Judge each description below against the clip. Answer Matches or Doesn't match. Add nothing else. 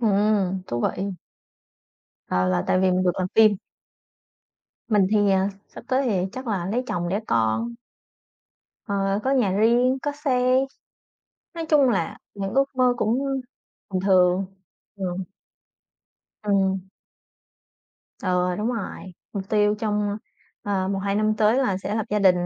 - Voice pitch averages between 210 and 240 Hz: Doesn't match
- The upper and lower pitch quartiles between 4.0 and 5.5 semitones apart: Doesn't match